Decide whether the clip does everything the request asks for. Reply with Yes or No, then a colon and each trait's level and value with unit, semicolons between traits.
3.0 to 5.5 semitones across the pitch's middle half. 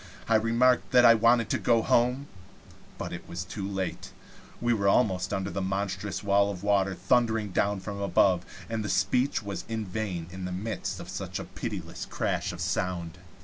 Yes: average, 3.4 semitones